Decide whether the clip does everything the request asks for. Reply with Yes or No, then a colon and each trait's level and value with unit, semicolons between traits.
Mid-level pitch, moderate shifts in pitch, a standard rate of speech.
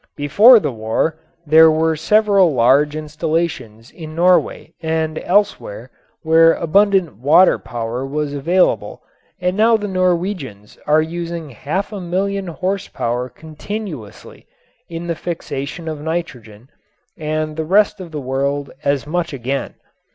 No: medium, 160 Hz; average, 4.3 semitones; slow, 130 wpm